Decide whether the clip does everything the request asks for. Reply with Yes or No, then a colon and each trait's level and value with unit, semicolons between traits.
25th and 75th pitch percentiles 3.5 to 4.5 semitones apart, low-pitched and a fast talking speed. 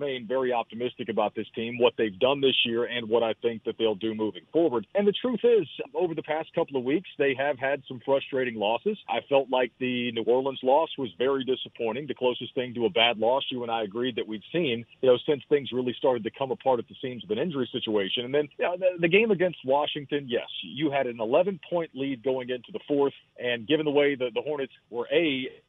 Yes: average, 3.8 semitones; low, 130 Hz; fast, 245 wpm